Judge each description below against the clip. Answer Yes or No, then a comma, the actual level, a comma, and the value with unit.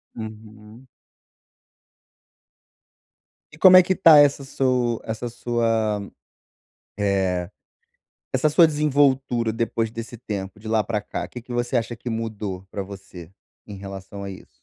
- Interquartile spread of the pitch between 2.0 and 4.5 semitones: Yes, average, 3.6 semitones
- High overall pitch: No, low, 115 Hz